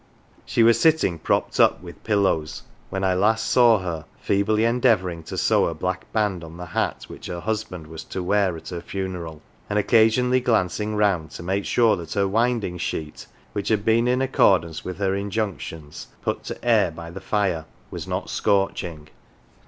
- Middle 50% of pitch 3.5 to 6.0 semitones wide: Yes, average, 4.3 semitones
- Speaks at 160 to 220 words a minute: Yes, average, 190 wpm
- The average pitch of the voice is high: No, very low, 95 Hz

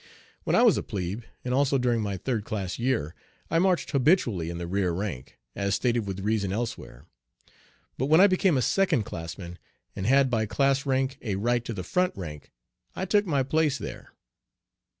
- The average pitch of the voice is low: Yes, low, 120 Hz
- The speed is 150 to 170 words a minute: No, average, 190 wpm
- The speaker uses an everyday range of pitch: No, wide, 6.1 semitones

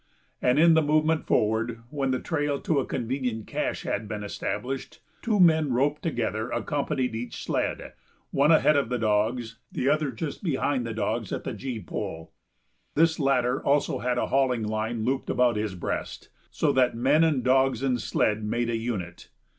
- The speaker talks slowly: No, average, 180 wpm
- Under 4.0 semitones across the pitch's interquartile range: No, average, 4.3 semitones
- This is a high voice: No, low, 125 Hz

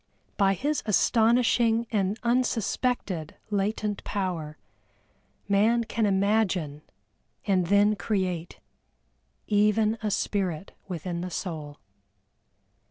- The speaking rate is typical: No, slow, 90 wpm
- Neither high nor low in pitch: No, high, 200 Hz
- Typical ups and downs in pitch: Yes, average, 3.4 semitones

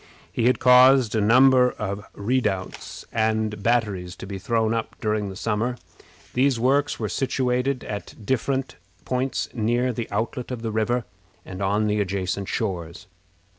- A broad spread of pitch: No, average, 3.4 semitones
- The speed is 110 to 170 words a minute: Yes, average, 150 wpm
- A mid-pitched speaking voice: No, low, 115 Hz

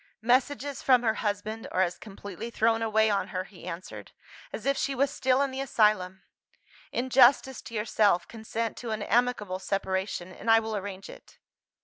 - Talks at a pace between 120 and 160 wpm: No, average, 175 wpm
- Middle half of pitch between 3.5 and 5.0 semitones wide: Yes, average, 3.9 semitones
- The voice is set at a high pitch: Yes, high, 220 Hz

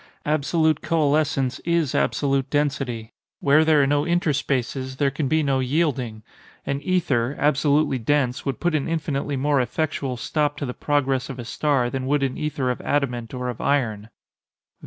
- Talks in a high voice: No, medium, 140 Hz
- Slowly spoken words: No, average, 165 wpm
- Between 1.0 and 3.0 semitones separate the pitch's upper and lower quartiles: Yes, narrow, 2.6 semitones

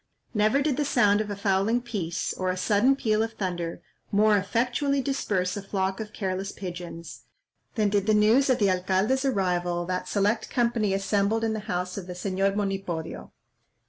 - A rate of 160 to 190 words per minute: Yes, average, 175 wpm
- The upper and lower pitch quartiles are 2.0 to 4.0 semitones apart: Yes, average, 3.2 semitones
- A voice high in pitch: Yes, high, 200 Hz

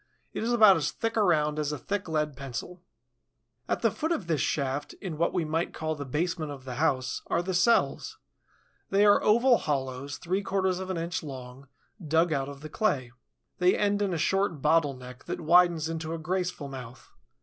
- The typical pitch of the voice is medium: Yes, medium, 160 Hz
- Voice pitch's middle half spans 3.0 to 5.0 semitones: Yes, average, 4.6 semitones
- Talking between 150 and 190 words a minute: No, average, 200 wpm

